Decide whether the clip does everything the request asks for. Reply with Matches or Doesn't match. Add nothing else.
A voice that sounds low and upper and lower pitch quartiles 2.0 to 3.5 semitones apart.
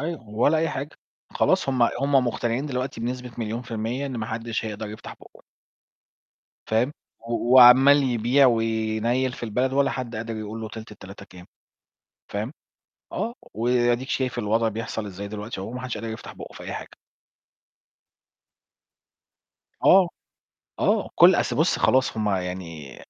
Matches